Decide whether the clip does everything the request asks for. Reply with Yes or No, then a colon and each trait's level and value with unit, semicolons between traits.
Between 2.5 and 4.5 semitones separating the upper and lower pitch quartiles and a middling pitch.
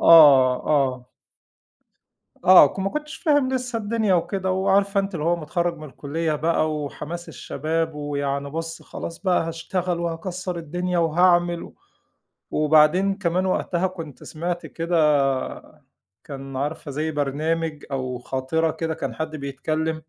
Yes: average, 3.3 semitones; medium, 165 Hz